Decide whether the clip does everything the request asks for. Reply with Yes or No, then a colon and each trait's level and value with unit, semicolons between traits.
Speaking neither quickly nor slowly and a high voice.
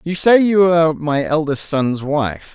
No: average, 190 wpm; medium, 155 Hz